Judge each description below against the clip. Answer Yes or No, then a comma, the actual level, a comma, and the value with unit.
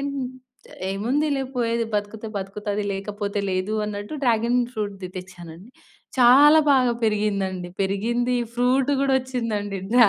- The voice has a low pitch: No, high, 215 Hz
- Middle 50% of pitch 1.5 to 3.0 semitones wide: No, average, 3.7 semitones